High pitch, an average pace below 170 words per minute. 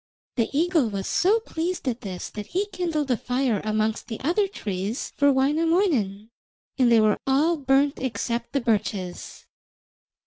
Yes: very high, 260 Hz; average, 150 wpm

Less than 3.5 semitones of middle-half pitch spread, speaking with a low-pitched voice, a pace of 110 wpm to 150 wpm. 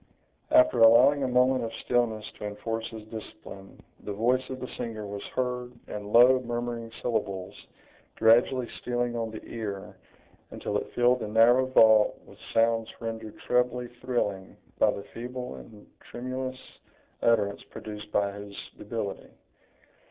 Yes: narrow, 2.6 semitones; low, 115 Hz; average, 140 wpm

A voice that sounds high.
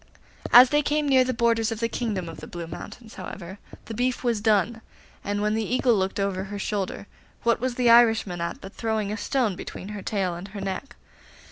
Yes: high, 215 Hz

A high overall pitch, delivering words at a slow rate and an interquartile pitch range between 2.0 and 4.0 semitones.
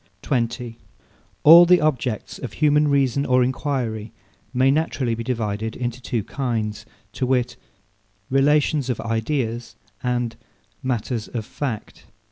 No: low, 125 Hz; slow, 120 wpm; average, 3.3 semitones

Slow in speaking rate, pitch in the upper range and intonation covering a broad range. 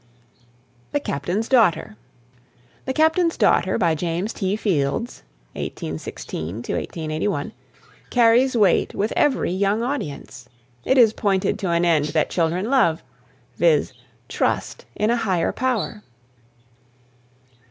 Yes: slow, 110 wpm; high, 195 Hz; wide, 6.4 semitones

